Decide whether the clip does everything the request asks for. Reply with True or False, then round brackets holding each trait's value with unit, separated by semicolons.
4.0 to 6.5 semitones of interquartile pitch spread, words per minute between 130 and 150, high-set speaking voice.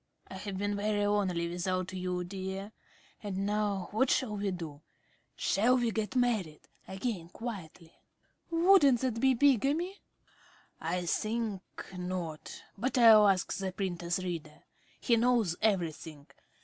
True (4.4 semitones; 140 wpm; 200 Hz)